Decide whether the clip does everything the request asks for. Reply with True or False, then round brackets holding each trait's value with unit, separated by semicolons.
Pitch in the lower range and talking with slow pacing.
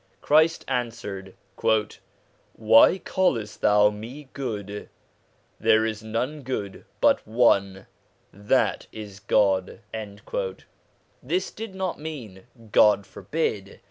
True (110 Hz; 100 wpm)